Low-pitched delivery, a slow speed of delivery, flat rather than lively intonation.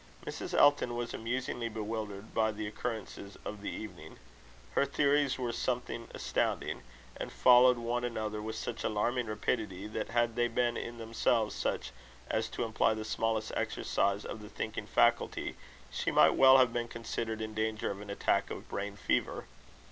No: low, 115 Hz; average, 165 wpm; narrow, 2.1 semitones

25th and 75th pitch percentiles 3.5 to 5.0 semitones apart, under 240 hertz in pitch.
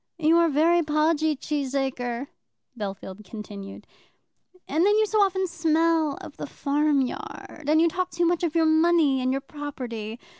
No: average, 4.1 semitones; very high, 305 Hz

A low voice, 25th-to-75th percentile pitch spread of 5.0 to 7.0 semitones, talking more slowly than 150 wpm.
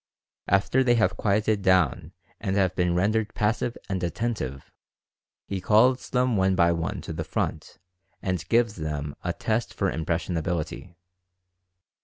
No: very low, 95 Hz; average, 4.3 semitones; average, 140 wpm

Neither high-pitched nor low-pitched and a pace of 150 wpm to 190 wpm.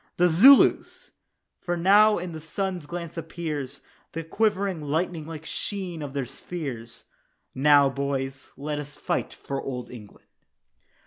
No: medium, 160 Hz; slow, 135 wpm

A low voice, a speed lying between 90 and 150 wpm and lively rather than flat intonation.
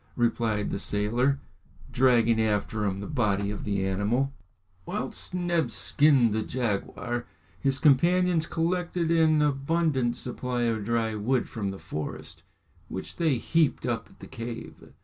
Yes: low, 120 Hz; average, 140 wpm; wide, 5.9 semitones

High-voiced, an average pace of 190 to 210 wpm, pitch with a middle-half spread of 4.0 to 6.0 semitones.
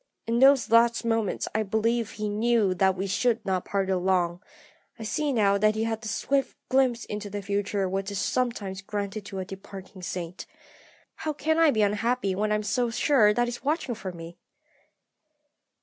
No: high, 210 Hz; average, 195 wpm; average, 3.5 semitones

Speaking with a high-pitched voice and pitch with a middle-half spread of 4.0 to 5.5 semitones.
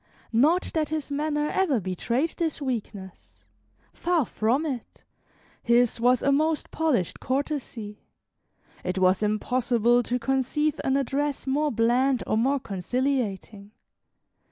Yes: very high, 255 Hz; average, 4.6 semitones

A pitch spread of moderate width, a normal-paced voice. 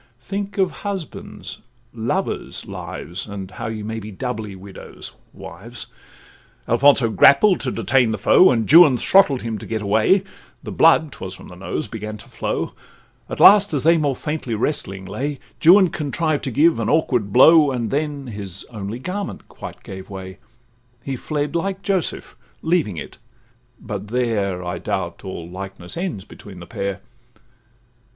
No: wide, 7.7 semitones; average, 155 wpm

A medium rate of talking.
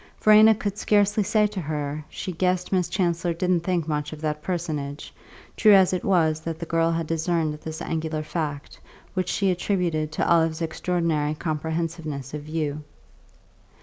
Yes: average, 160 wpm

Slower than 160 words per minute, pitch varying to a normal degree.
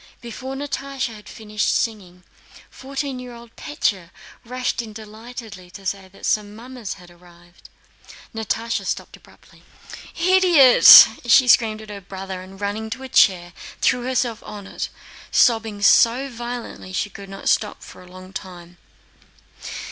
Yes: average, 150 wpm; average, 4.3 semitones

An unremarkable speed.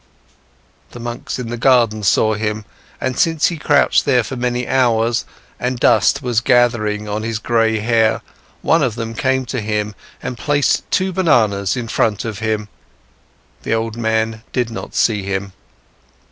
Yes: average, 160 wpm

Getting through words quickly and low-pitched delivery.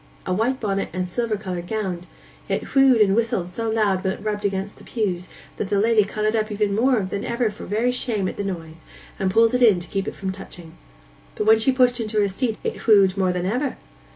No: fast, 235 wpm; high, 210 Hz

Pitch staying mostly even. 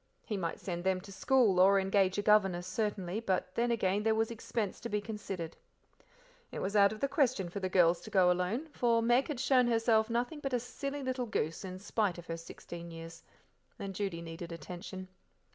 No: average, 4.3 semitones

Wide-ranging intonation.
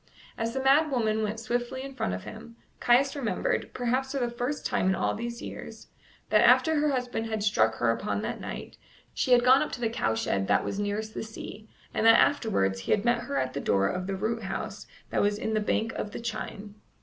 No: average, 3.4 semitones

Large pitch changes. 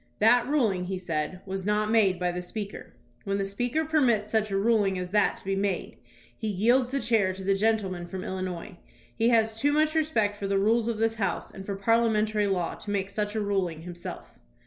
No: average, 2.9 semitones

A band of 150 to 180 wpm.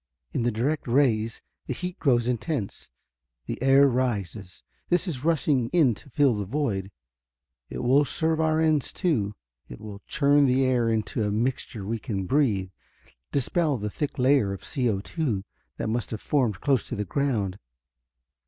Yes: average, 160 wpm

